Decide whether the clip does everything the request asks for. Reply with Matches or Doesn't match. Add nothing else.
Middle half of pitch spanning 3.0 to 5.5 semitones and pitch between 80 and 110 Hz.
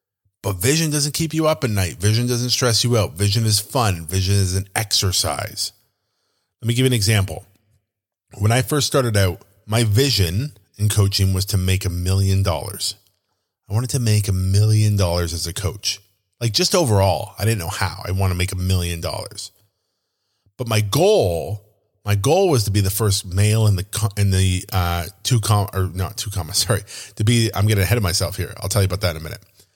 Doesn't match